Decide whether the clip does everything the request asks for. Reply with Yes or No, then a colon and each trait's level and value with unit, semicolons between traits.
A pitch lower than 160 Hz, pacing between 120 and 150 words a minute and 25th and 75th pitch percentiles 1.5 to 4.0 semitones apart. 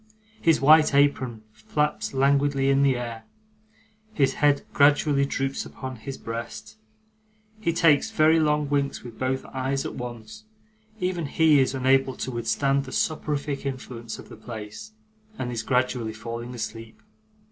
Yes: low, 135 Hz; average, 145 wpm; average, 3.4 semitones